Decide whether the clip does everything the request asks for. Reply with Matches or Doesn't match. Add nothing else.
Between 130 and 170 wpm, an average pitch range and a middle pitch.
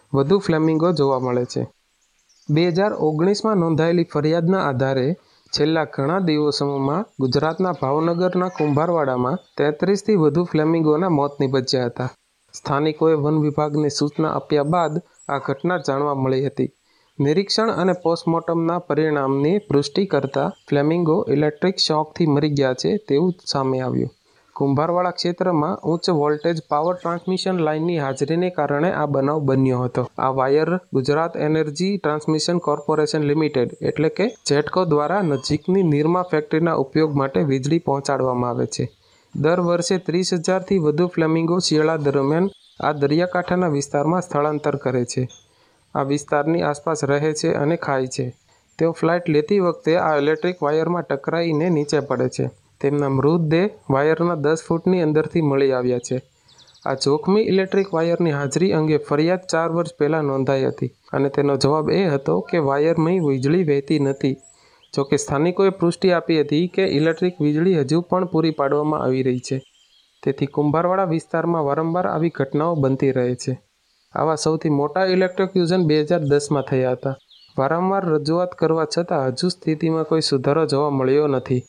Matches